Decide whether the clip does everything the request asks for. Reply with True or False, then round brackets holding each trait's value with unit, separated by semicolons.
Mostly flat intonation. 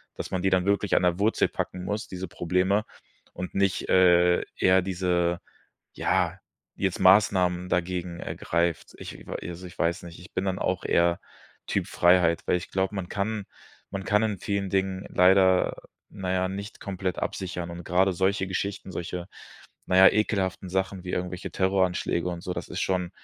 True (1.4 semitones)